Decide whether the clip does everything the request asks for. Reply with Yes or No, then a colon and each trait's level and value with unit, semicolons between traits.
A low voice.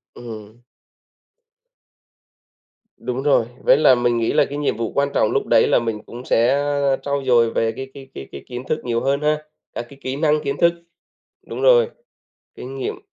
Yes: low, 130 Hz